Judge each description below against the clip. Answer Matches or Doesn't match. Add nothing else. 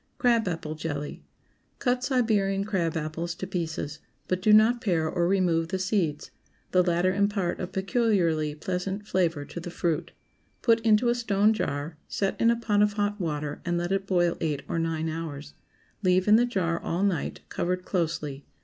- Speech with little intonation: Doesn't match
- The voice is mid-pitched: Matches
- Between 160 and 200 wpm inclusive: Matches